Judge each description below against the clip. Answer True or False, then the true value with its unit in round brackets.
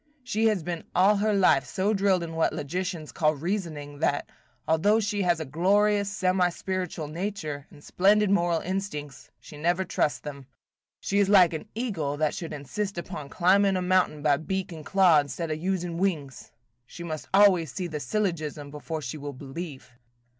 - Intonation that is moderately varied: True (4.3 semitones)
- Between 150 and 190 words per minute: True (175 wpm)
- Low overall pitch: False (175 Hz)